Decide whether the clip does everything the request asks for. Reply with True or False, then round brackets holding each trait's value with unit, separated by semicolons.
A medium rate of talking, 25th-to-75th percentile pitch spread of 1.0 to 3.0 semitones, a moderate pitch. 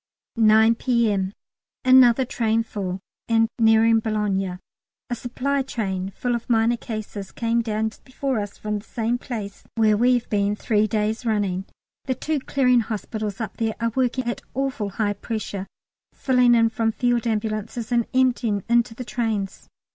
False (155 wpm; 2.4 semitones; 225 Hz)